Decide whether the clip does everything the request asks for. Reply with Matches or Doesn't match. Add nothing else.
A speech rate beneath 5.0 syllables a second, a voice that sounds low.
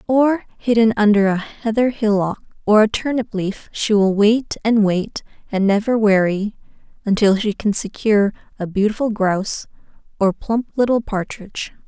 Doesn't match